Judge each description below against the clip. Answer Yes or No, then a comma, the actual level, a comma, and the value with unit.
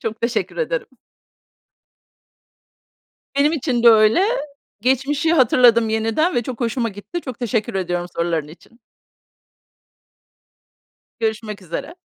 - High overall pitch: Yes, high, 230 Hz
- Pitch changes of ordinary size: Yes, average, 3.7 semitones